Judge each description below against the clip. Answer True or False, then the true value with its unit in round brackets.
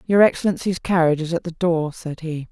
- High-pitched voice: False (170 Hz)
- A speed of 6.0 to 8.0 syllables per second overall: False (5.8 syllables/s)